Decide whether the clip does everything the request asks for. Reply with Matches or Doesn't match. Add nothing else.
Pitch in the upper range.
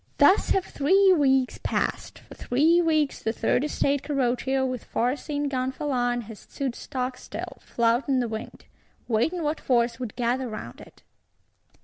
Matches